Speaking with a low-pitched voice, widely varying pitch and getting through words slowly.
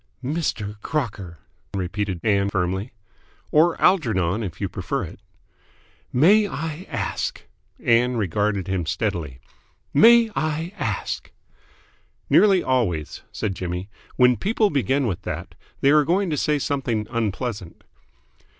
Yes: low, 115 Hz; wide, 8.0 semitones; slow, 125 wpm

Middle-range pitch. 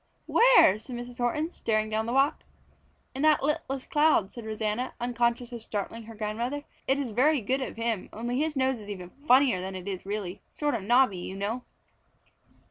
No: high, 235 Hz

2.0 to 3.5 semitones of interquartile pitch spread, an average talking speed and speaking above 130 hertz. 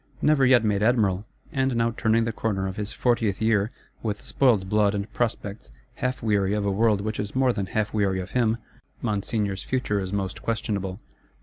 No: narrow, 2.6 semitones; average, 190 wpm; low, 105 Hz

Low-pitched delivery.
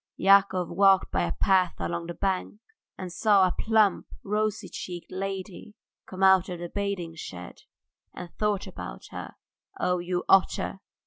No: high, 190 Hz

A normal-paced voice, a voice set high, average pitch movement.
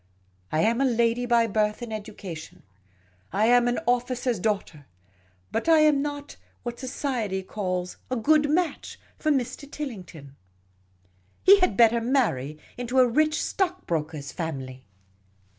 No: average, 155 wpm; high, 235 Hz; wide, 6.5 semitones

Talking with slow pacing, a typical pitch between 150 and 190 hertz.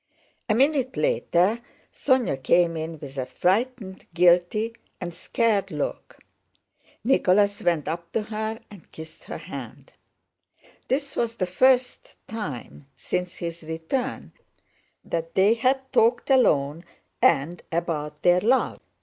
Yes: slow, 125 wpm; medium, 185 Hz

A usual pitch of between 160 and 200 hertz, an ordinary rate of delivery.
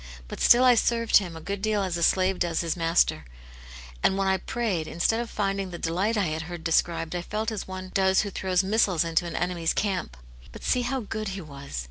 No: high, 190 Hz; fast, 225 wpm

